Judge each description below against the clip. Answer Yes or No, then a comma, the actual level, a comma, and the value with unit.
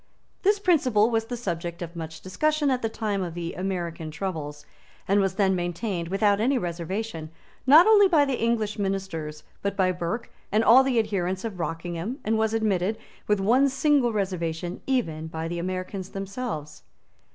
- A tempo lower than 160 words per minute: No, average, 170 wpm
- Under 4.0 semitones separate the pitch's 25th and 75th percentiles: No, average, 4.9 semitones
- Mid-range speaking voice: No, high, 195 Hz